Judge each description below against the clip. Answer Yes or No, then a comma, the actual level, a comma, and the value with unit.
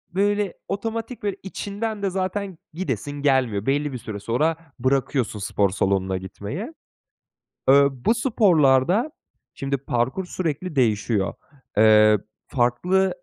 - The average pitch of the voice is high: No, medium, 140 Hz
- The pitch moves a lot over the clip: Yes, wide, 8.8 semitones